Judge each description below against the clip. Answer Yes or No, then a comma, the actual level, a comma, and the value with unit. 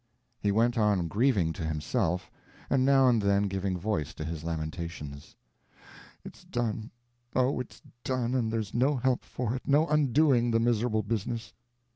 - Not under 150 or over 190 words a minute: Yes, average, 155 wpm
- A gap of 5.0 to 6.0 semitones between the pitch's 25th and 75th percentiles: Yes, wide, 5.6 semitones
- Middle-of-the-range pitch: No, low, 110 Hz